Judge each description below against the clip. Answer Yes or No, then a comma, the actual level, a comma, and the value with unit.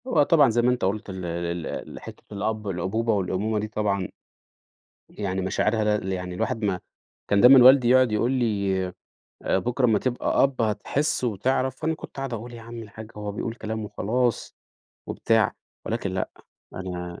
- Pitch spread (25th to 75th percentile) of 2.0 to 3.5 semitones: No, average, 4.0 semitones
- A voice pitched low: Yes, low, 110 Hz